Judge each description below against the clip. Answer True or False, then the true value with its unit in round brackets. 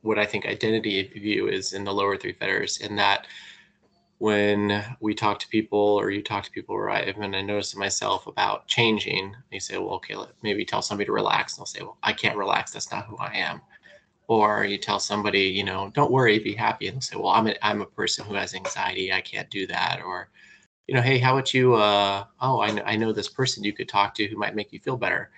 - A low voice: True (105 Hz)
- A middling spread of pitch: False (1.6 semitones)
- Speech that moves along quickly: True (245 wpm)